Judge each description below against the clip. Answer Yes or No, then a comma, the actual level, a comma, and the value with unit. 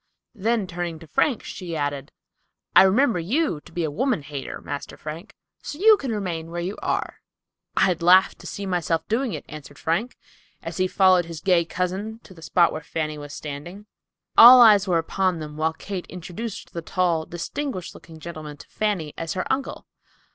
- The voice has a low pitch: No, medium, 175 Hz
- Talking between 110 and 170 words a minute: No, average, 185 wpm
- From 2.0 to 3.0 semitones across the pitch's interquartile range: No, average, 4.2 semitones